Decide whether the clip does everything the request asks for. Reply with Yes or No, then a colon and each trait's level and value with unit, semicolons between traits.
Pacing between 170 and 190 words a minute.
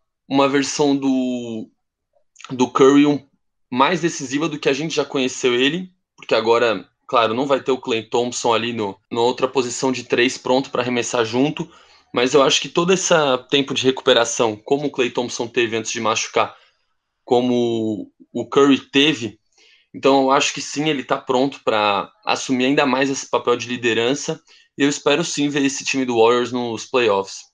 Yes: average, 180 wpm